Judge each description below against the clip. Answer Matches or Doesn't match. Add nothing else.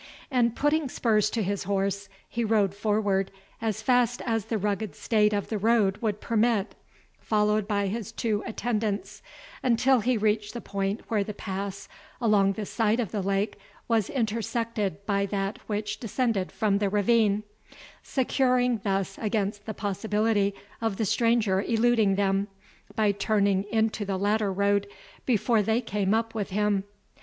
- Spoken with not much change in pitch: Matches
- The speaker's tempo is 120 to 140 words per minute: Doesn't match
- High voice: Matches